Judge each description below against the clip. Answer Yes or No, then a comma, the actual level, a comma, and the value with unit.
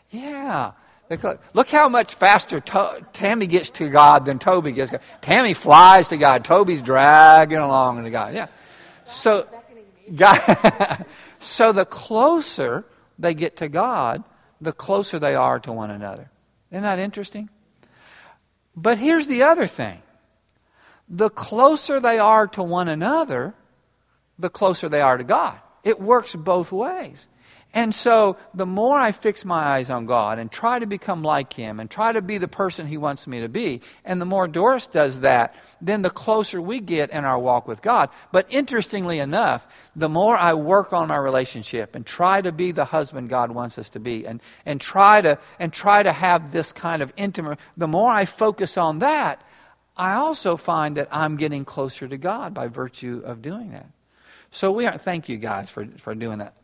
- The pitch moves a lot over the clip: Yes, wide, 7.0 semitones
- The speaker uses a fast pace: No, average, 180 wpm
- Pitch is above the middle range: No, medium, 175 Hz